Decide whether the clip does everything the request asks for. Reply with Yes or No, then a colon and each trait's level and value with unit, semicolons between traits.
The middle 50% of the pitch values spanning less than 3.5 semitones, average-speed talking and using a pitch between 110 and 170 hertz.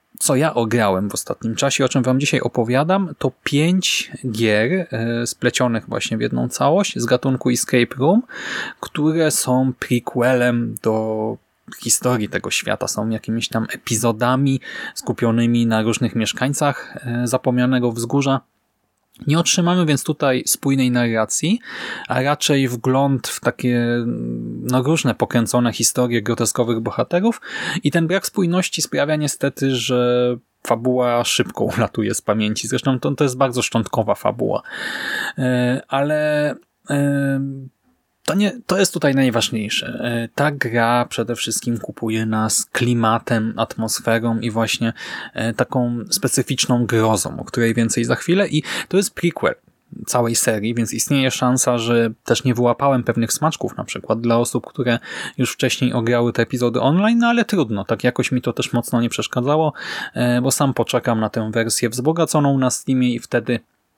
Yes: average, 2.9 semitones; average, 140 wpm; low, 125 Hz